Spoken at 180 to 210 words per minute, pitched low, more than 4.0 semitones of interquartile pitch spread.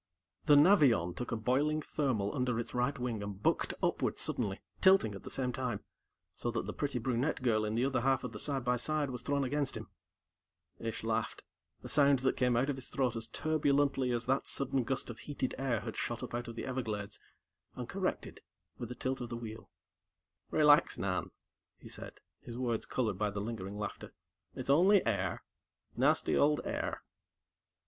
No: average, 190 wpm; low, 125 Hz; average, 3.5 semitones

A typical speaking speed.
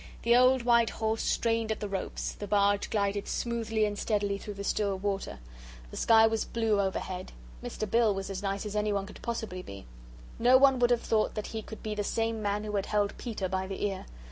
No: fast, 220 wpm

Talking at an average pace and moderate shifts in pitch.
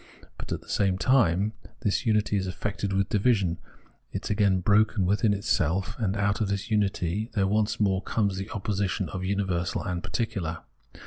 No: average, 170 wpm; narrow, 2.1 semitones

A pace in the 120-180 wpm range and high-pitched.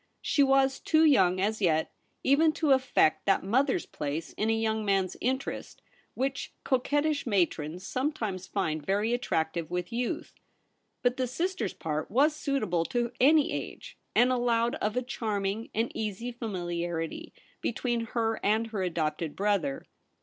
Yes: average, 150 wpm; high, 225 Hz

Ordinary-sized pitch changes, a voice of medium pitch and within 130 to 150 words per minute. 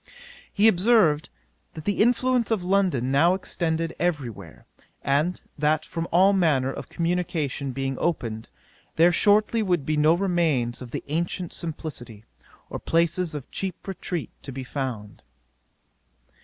Yes: average, 4.8 semitones; medium, 165 Hz; average, 140 wpm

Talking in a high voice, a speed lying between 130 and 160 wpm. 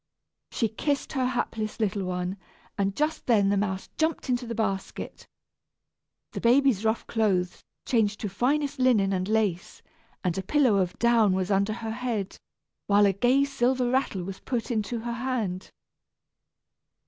Yes: high, 220 Hz; average, 155 wpm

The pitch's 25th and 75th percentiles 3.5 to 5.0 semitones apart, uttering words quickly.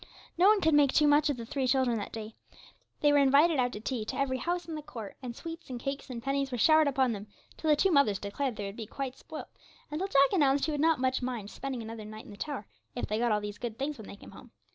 Yes: average, 4.5 semitones; fast, 285 wpm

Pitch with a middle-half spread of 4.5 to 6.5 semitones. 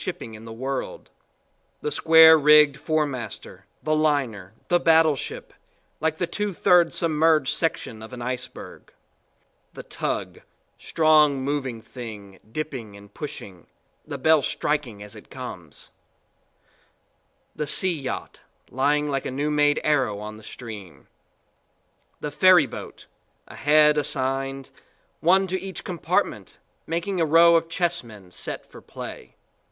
Yes: average, 4.8 semitones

